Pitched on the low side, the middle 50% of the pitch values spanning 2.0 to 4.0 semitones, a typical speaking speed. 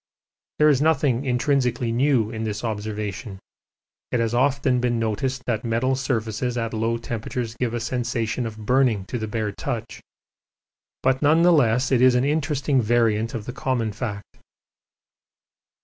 Yes: low, 120 Hz; average, 2.7 semitones; average, 155 wpm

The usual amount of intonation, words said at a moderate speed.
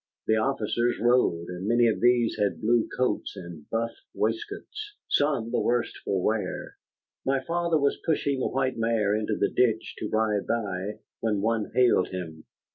Yes: average, 3.3 semitones; average, 165 wpm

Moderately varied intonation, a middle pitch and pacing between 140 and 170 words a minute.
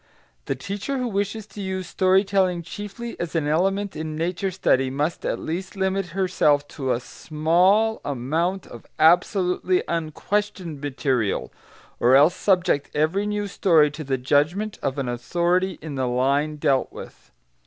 Yes: average, 5.0 semitones; medium, 170 Hz; average, 155 wpm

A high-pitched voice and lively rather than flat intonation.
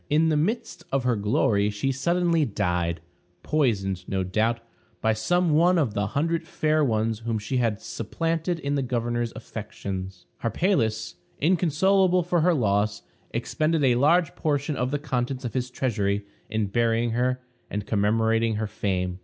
No: low, 120 Hz; wide, 6.6 semitones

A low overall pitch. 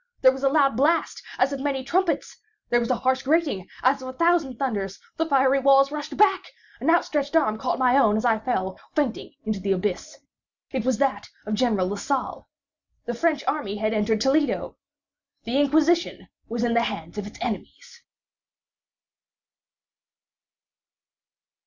No: very high, 260 Hz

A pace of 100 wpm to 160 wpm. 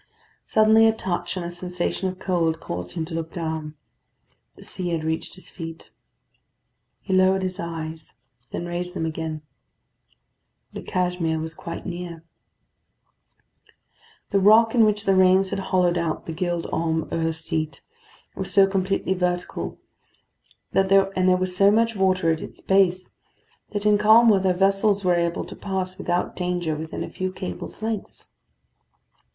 Yes: average, 155 wpm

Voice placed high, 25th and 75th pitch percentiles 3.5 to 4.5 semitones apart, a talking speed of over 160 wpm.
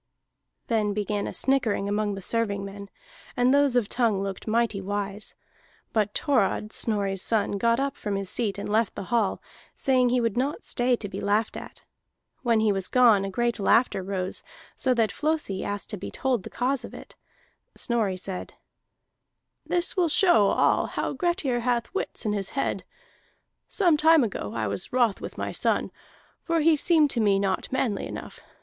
Yes: high, 220 Hz; average, 4.1 semitones; average, 180 wpm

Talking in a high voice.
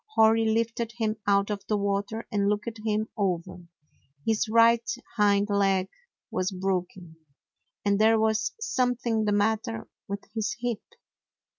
Yes: high, 215 Hz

